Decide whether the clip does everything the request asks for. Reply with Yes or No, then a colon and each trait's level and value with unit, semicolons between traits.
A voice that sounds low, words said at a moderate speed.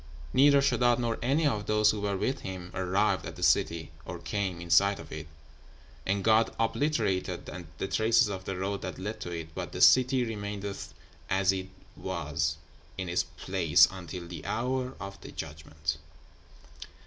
Yes: low, 100 Hz; average, 170 wpm